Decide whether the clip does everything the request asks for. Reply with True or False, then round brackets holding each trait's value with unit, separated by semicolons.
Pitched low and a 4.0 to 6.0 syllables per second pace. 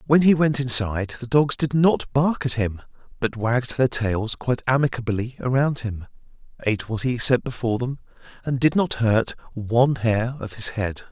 True (120 Hz; 5.0 syllables/s)